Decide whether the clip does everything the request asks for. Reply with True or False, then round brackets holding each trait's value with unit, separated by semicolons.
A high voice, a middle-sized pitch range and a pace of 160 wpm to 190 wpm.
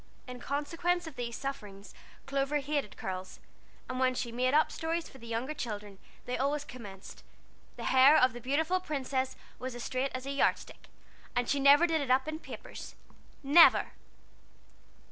True (265 Hz; 3.3 semitones; 170 wpm)